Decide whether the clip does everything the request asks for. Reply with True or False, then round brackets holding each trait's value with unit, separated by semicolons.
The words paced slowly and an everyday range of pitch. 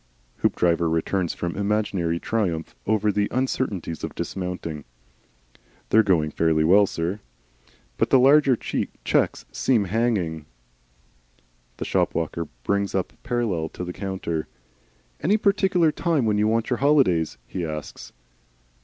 False (130 wpm; 6.0 semitones)